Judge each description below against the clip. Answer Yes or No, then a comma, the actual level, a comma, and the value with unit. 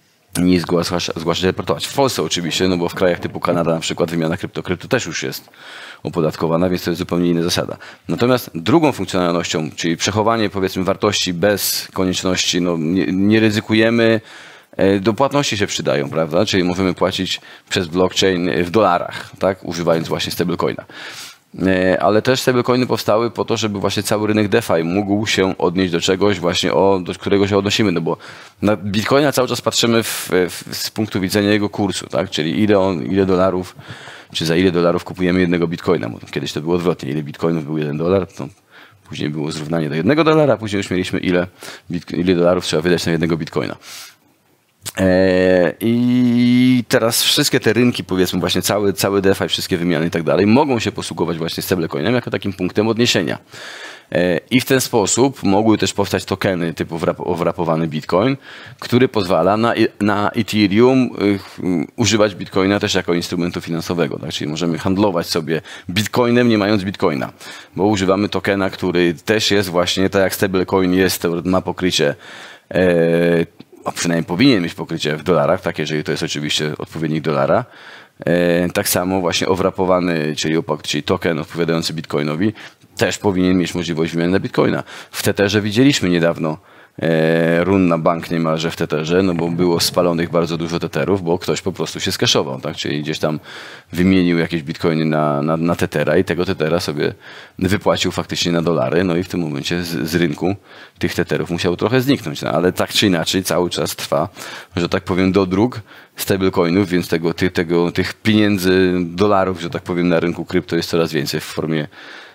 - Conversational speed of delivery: No, fast, 175 wpm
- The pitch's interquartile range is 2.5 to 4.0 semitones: Yes, average, 3.2 semitones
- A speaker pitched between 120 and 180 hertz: No, very low, 90 Hz